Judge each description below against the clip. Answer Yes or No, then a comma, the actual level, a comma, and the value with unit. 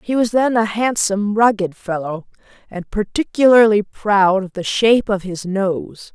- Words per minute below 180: Yes, average, 155 wpm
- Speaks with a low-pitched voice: No, high, 205 Hz